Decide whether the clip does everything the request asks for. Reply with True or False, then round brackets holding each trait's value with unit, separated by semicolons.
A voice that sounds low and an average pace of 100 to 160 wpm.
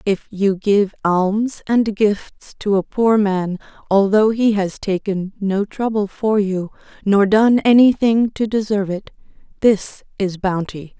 False (205 Hz; 145 wpm)